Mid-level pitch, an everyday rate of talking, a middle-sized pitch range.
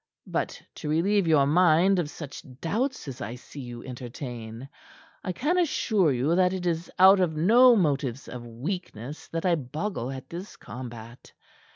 No: medium, 155 Hz; average, 165 wpm; wide, 6.6 semitones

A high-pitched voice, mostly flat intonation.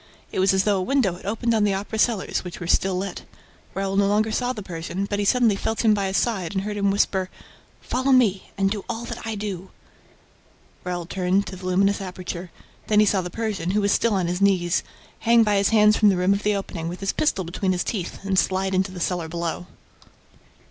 Yes: high, 195 Hz; narrow, 2.3 semitones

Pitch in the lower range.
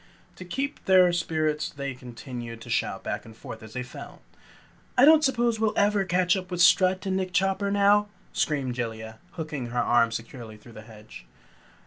No: medium, 160 Hz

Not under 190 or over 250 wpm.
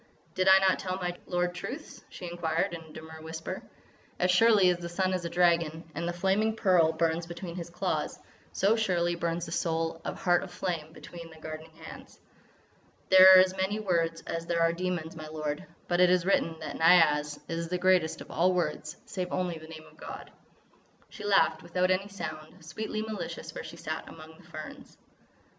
Yes: average, 195 wpm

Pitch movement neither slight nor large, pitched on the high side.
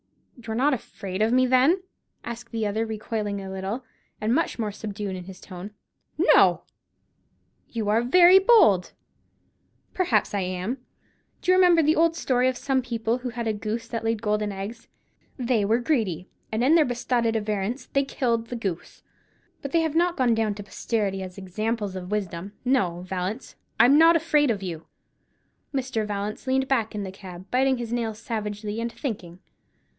Yes: average, 4.1 semitones; high, 225 Hz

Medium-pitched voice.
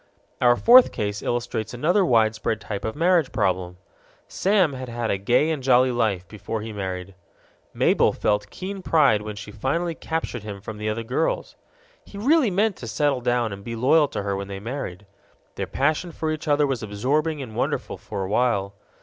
No: low, 120 Hz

